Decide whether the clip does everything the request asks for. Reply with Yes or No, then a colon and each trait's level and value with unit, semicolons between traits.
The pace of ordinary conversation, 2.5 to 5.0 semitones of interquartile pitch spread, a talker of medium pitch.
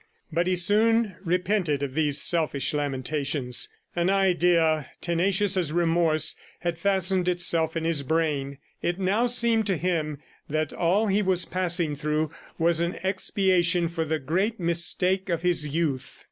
Yes: average, 145 wpm; average, 3.1 semitones; medium, 170 Hz